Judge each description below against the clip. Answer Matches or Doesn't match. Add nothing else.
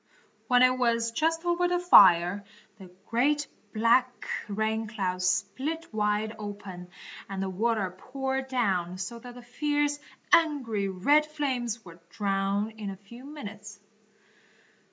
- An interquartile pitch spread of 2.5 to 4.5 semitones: Doesn't match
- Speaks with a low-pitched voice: Doesn't match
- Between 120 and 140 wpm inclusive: Matches